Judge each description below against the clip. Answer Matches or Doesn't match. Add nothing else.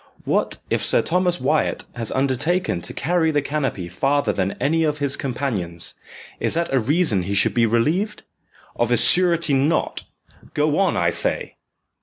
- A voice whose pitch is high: Doesn't match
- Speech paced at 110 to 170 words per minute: Matches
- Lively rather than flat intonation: Matches